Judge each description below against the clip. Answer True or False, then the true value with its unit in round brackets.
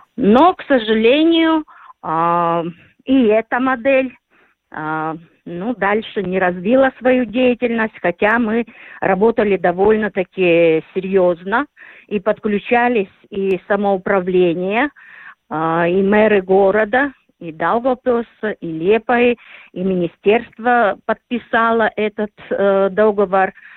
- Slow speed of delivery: True (85 wpm)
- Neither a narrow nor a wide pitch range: True (4.4 semitones)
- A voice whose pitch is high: True (210 Hz)